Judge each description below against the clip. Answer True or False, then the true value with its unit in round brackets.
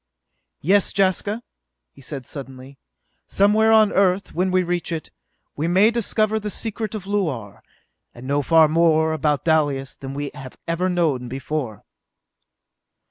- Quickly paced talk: False (140 wpm)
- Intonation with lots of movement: True (6.0 semitones)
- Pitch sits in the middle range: True (165 Hz)